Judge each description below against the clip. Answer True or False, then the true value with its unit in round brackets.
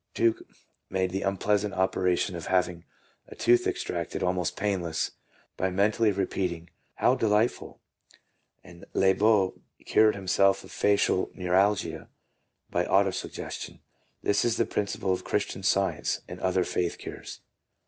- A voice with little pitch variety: True (2.1 semitones)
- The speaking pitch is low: True (95 Hz)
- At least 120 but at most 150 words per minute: True (135 wpm)